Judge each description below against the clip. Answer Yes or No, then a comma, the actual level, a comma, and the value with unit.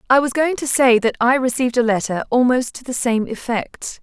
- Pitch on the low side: No, very high, 250 Hz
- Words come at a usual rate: No, fast, 225 wpm